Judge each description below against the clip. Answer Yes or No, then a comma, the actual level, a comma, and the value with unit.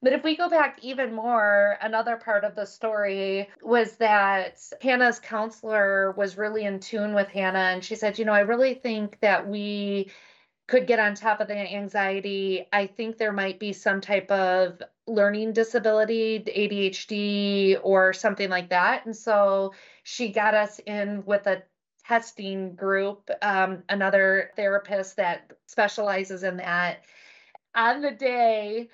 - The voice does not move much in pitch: Yes, narrow, 2.3 semitones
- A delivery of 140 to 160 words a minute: Yes, average, 155 wpm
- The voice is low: No, high, 205 Hz